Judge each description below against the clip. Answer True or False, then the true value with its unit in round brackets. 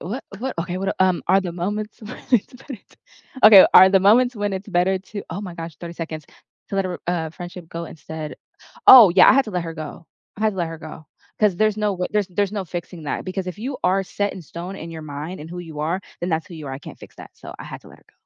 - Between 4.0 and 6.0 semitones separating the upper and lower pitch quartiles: False (3.4 semitones)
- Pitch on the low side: False (185 Hz)